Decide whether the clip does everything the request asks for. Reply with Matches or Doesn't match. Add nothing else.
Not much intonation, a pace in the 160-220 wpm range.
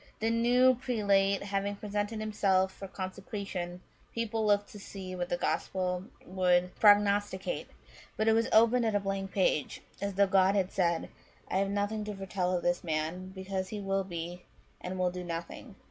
Matches